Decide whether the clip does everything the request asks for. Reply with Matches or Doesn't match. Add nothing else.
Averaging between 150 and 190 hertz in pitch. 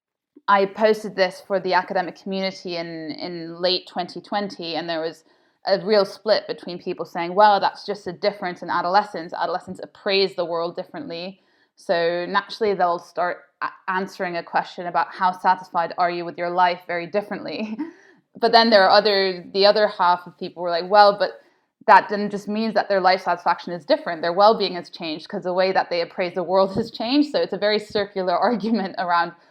Matches